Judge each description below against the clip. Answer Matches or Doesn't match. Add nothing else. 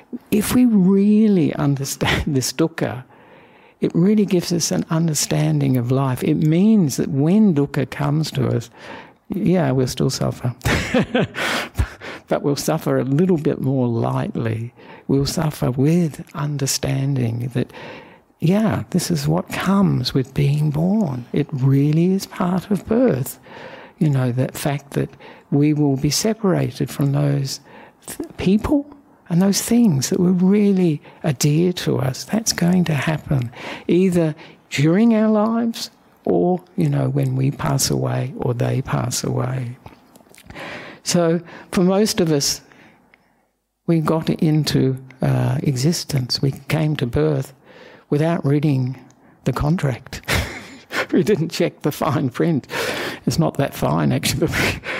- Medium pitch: Matches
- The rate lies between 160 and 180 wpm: Doesn't match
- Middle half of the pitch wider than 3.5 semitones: Matches